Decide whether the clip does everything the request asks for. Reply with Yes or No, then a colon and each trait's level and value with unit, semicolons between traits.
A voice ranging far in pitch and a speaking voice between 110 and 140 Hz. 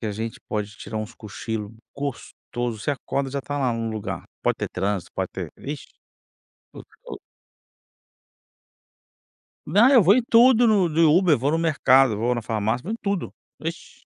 Yes: wide, 7.1 semitones; low, 135 Hz